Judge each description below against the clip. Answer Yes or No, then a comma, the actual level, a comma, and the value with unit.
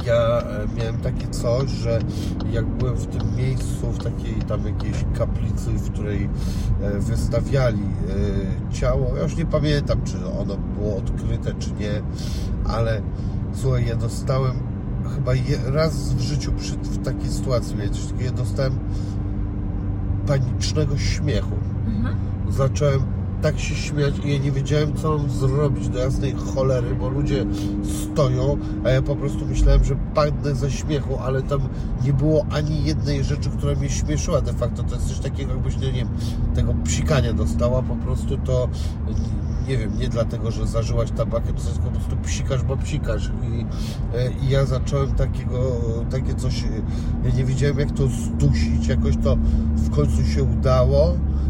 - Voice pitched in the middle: No, low, 110 Hz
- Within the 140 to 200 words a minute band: Yes, average, 150 wpm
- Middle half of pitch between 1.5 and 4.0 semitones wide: No, average, 4.6 semitones